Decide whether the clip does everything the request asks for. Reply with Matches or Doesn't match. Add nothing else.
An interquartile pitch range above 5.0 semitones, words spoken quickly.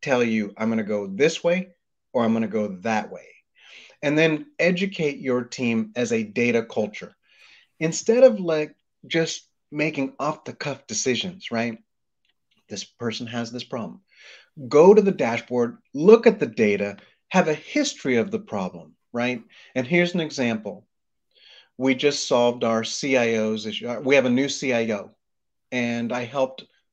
Doesn't match